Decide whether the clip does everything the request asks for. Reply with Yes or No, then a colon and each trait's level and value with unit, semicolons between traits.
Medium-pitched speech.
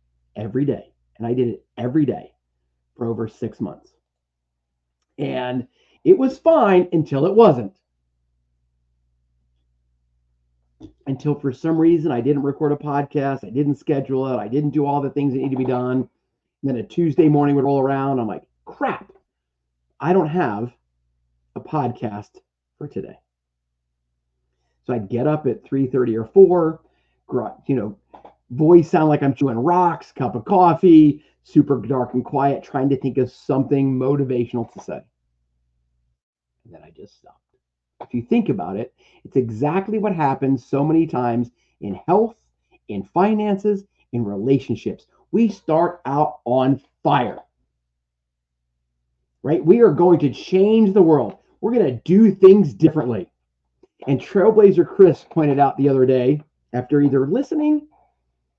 No: low, 130 Hz